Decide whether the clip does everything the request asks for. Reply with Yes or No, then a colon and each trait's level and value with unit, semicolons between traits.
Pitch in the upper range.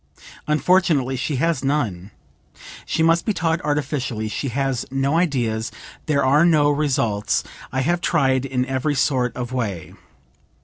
No: low, 135 Hz